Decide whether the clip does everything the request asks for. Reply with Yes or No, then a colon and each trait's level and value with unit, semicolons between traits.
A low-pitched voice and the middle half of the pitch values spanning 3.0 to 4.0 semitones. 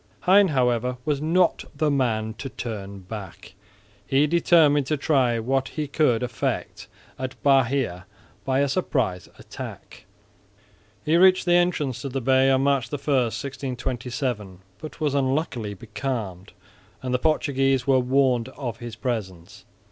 Yes: low, 130 Hz; average, 3.6 semitones